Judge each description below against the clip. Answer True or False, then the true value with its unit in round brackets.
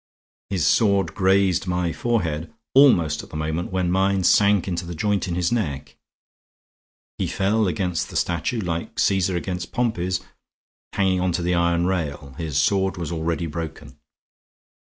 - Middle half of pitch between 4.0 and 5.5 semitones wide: False (2.5 semitones)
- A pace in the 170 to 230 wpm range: False (155 wpm)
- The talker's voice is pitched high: False (90 Hz)